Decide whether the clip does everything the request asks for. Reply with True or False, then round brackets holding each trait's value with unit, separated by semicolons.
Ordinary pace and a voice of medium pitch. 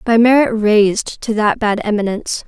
False (170 wpm; 215 Hz)